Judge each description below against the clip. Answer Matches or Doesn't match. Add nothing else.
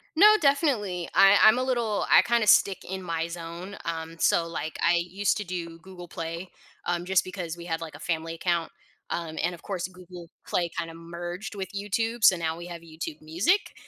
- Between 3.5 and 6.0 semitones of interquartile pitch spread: Doesn't match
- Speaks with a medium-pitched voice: Matches